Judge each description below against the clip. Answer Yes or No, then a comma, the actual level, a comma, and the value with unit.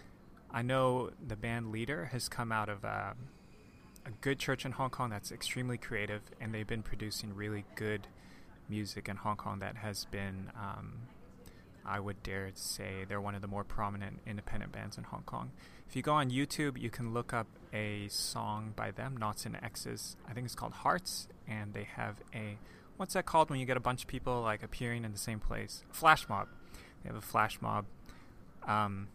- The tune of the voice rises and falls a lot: No, average, 3.3 semitones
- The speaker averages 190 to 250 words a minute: Yes, average, 200 wpm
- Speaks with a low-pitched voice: Yes, low, 110 Hz